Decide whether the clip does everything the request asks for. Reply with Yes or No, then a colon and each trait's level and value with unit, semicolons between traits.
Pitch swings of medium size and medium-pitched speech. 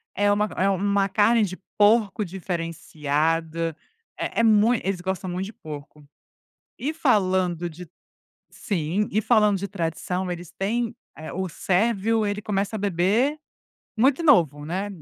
No: average, 3.7 semitones; high, 195 Hz